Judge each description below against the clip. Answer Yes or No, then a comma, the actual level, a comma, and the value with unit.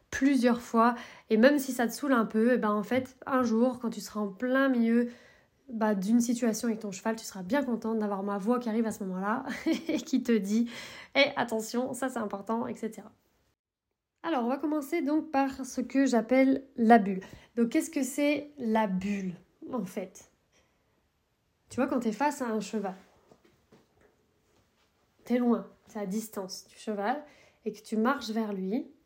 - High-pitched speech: Yes, high, 235 Hz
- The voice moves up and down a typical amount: Yes, average, 3.5 semitones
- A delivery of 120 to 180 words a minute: No, average, 190 wpm